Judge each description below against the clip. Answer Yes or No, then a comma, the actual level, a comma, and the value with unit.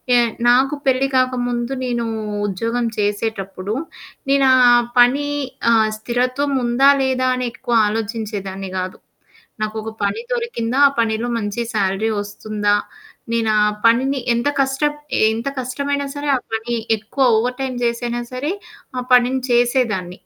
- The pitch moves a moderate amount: Yes, average, 3.1 semitones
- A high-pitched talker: Yes, high, 240 Hz